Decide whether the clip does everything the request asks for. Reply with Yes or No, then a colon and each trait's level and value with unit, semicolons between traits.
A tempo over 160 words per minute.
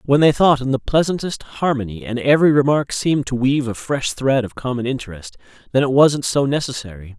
Yes: average, 200 wpm